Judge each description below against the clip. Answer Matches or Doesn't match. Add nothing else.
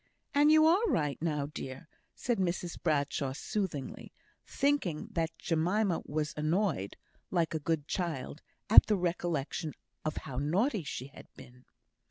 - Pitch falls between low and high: Matches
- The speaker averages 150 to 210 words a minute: Doesn't match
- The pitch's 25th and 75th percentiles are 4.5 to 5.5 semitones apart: Matches